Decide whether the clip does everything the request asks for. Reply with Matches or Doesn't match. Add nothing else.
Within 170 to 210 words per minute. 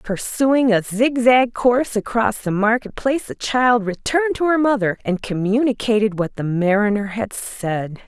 Doesn't match